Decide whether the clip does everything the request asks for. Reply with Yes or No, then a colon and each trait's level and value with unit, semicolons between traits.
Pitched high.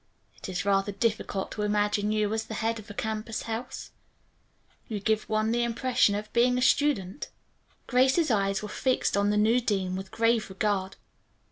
Yes: high, 215 Hz